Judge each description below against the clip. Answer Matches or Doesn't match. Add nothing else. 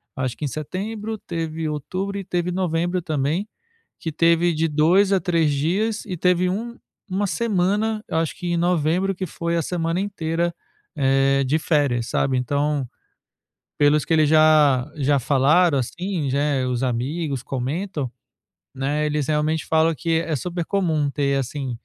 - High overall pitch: Doesn't match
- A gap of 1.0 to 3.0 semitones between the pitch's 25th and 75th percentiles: Doesn't match